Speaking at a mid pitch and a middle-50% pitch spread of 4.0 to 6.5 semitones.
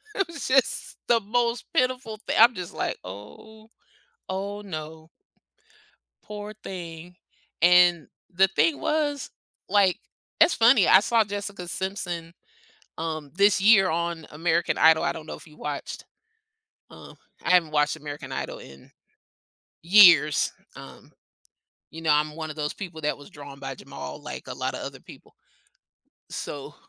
Yes: medium, 175 Hz; average, 4.9 semitones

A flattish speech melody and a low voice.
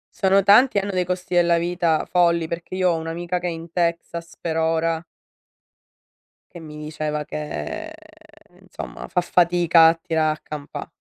No: narrow, 1.7 semitones; medium, 170 Hz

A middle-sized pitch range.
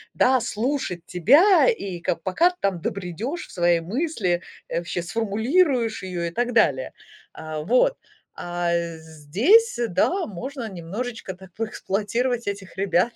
No: wide, 6.3 semitones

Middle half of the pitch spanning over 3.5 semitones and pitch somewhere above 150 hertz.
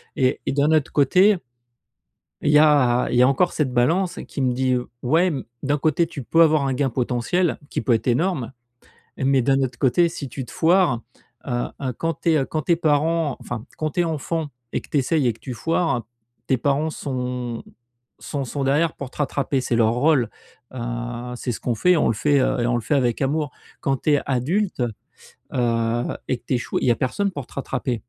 No: average, 4.1 semitones; low, 135 Hz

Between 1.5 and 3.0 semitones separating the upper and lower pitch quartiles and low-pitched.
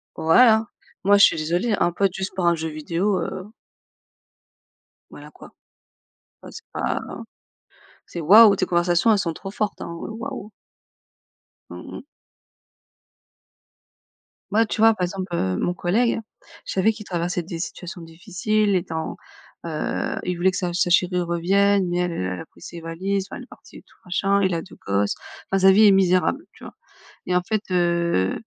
No: average, 2.7 semitones; medium, 180 Hz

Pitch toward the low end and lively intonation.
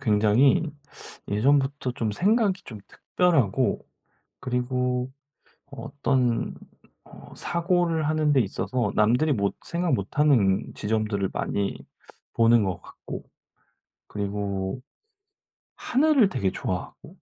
Yes: low, 125 Hz; wide, 6.7 semitones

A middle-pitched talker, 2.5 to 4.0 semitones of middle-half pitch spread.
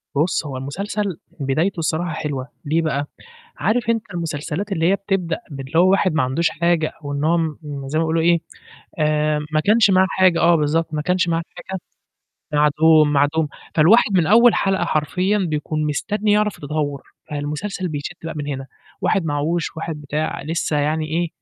Yes: medium, 160 Hz; average, 3.4 semitones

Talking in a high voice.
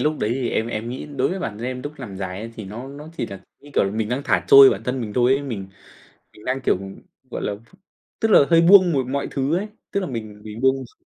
No: low, 125 Hz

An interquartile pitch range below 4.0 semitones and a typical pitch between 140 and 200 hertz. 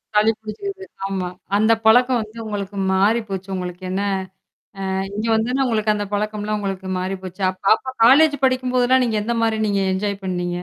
No: average, 3.4 semitones; high, 210 Hz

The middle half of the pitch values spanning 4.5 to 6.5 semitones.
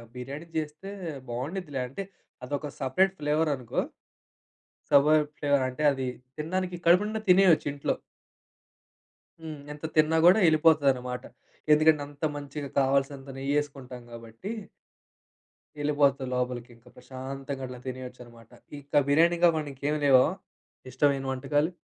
No: average, 3.0 semitones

